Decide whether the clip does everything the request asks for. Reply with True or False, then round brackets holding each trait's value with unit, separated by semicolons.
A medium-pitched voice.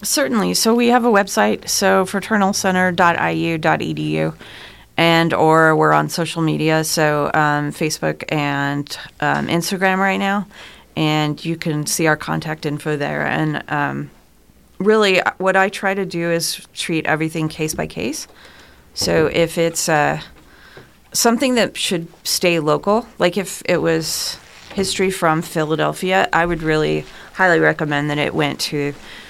True (165 Hz)